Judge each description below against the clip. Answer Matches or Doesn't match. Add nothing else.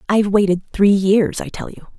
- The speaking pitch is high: Matches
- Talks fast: Matches